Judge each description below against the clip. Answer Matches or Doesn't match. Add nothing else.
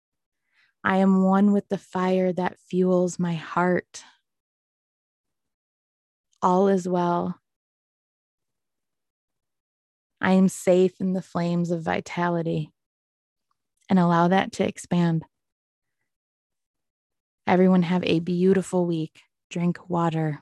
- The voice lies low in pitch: Doesn't match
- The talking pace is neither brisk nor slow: Doesn't match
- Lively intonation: Doesn't match